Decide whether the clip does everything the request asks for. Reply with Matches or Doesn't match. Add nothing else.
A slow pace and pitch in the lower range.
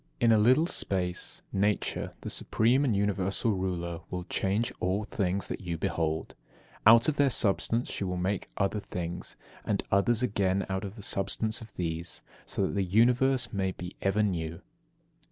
Doesn't match